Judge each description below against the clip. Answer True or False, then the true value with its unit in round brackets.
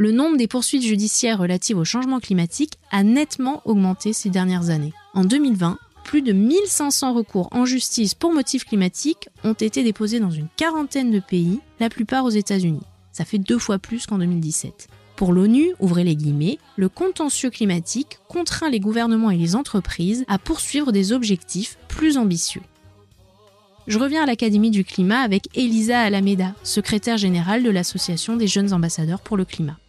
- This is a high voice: True (210 Hz)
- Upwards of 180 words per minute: False (170 wpm)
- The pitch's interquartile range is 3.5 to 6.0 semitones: True (5.1 semitones)